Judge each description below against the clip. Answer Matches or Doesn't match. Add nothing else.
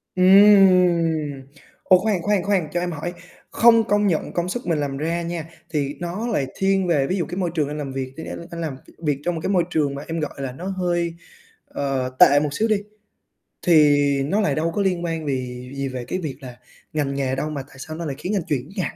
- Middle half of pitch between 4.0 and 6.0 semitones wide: Matches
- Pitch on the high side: Doesn't match